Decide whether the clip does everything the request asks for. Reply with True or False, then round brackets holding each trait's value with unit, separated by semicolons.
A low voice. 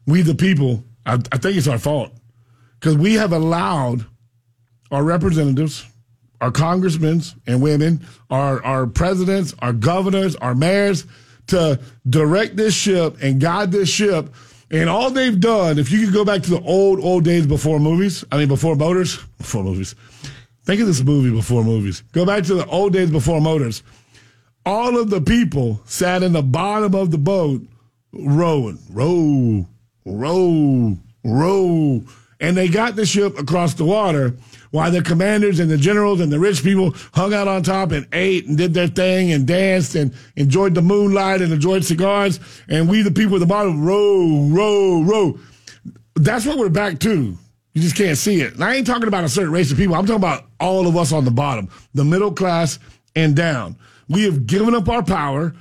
False (160 Hz)